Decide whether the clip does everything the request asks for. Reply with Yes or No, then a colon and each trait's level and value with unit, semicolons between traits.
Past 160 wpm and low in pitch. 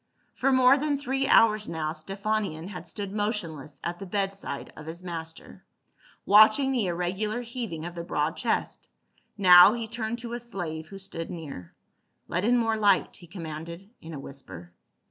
No: average, 170 wpm; high, 195 Hz